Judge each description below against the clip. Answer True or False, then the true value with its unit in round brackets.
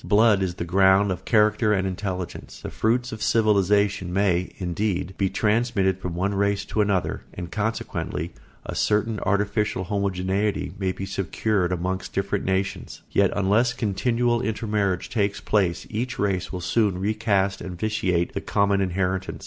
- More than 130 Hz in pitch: False (100 Hz)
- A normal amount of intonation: False (2.3 semitones)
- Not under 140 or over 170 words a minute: True (150 wpm)